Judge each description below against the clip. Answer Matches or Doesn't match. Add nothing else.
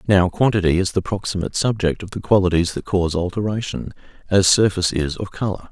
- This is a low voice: Matches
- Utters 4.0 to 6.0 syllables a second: Doesn't match